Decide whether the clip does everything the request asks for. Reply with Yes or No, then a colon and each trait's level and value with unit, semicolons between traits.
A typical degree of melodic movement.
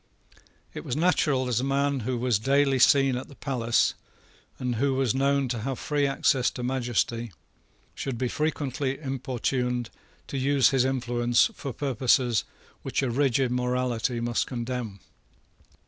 No: narrow, 2.2 semitones